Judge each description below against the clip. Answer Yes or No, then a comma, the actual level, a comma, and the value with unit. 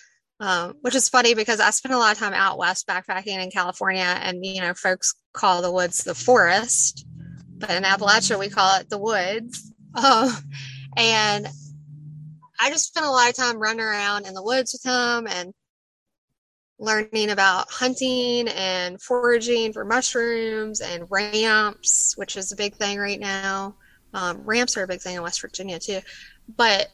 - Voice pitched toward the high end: Yes, high, 205 Hz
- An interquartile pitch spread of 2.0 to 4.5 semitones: Yes, average, 4.1 semitones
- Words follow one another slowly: No, average, 170 wpm